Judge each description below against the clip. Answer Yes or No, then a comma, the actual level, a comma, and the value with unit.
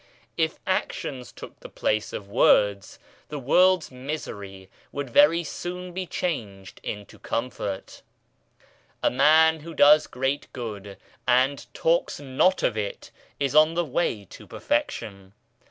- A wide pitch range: Yes, wide, 7.2 semitones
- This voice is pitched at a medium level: No, low, 130 Hz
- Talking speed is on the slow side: Yes, slow, 130 wpm